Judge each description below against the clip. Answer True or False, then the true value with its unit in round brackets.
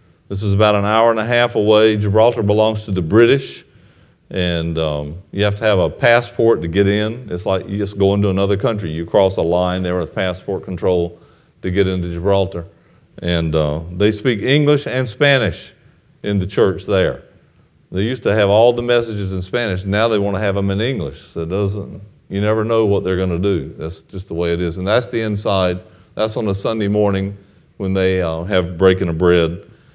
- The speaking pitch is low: True (100 Hz)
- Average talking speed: False (210 wpm)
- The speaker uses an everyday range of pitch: True (3.2 semitones)